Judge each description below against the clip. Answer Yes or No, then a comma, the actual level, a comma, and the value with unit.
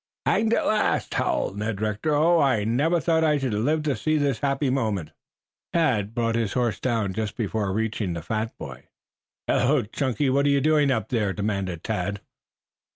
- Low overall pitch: Yes, low, 115 Hz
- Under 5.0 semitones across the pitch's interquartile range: No, wide, 5.4 semitones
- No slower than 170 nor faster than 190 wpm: Yes, average, 180 wpm